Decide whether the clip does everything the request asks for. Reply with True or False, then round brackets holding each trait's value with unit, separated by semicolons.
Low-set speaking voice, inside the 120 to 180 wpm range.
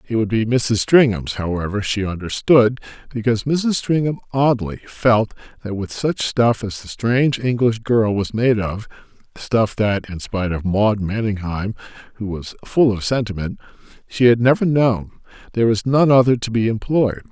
True (115 Hz; 165 wpm)